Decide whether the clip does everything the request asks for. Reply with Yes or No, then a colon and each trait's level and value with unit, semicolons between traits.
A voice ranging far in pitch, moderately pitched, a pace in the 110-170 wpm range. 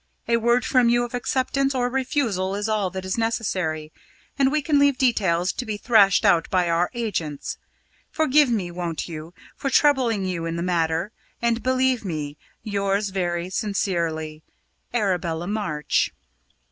No: wide, 5.8 semitones; high, 200 Hz; average, 155 wpm